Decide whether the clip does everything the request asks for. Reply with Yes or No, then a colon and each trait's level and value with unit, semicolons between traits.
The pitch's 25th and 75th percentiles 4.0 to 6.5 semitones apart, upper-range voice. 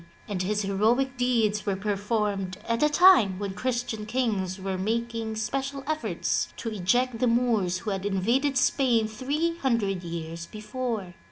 Yes: average, 4.3 semitones; high, 220 Hz